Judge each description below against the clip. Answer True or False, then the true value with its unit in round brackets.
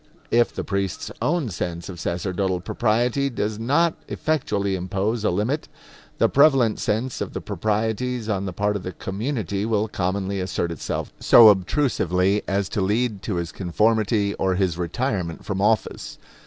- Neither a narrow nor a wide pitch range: True (3.6 semitones)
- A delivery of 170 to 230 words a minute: False (155 wpm)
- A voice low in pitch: True (105 Hz)